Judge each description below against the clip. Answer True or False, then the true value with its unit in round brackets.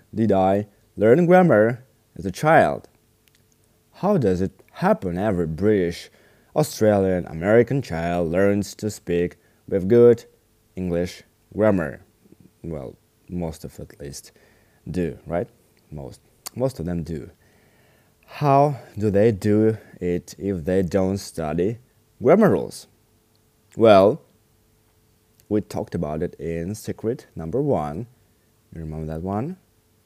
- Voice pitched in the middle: False (105 Hz)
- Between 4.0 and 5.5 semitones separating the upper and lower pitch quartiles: False (3.2 semitones)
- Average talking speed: False (120 wpm)